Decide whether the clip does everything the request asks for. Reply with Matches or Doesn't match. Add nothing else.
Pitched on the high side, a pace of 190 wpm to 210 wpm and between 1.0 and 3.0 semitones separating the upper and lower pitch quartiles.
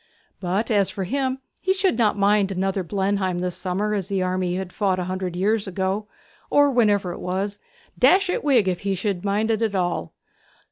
Matches